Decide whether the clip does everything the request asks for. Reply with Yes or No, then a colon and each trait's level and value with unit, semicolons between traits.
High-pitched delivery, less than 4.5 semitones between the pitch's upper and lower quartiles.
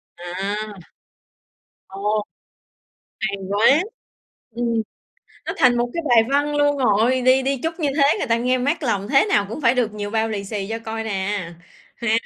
Yes: high, 230 Hz; average, 4.1 semitones